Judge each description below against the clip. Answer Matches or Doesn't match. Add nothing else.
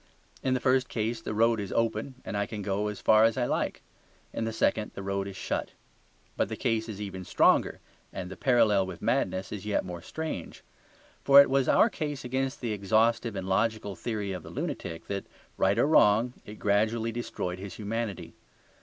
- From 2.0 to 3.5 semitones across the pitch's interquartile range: Matches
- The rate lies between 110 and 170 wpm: Doesn't match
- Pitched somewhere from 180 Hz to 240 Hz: Doesn't match